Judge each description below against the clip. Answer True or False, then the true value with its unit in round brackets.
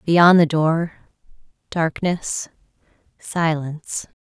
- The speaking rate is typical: False (70 wpm)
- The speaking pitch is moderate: True (165 Hz)